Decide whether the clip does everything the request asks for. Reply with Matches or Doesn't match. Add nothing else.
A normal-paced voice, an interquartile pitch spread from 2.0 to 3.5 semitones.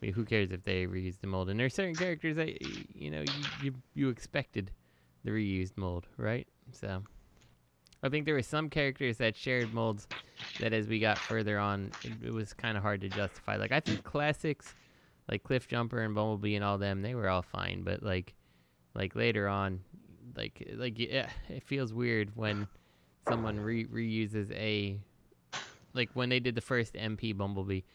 Doesn't match